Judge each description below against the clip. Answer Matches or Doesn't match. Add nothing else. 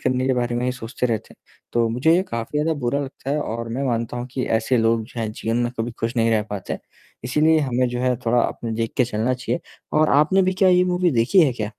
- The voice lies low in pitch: Matches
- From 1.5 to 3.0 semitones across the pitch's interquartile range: Doesn't match